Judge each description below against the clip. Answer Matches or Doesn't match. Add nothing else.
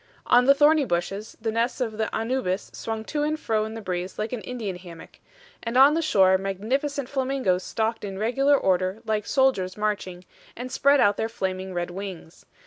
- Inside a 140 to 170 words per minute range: Doesn't match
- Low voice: Doesn't match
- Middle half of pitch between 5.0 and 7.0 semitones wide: Matches